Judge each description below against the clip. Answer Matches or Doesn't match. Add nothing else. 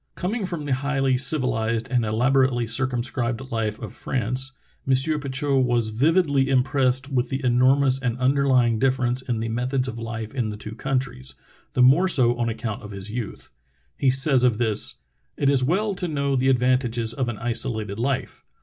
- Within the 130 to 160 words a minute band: Doesn't match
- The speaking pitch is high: Doesn't match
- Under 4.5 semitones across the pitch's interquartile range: Matches